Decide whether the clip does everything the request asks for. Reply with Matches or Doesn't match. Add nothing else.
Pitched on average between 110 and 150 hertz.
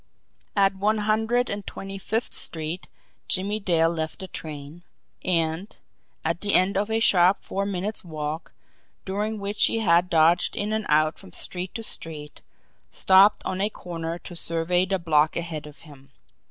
Doesn't match